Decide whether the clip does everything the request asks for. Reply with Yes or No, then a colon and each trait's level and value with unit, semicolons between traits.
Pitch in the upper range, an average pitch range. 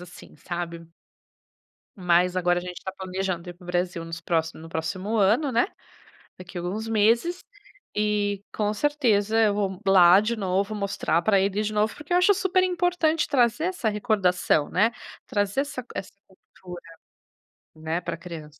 Yes: high, 200 Hz; average, 4.2 semitones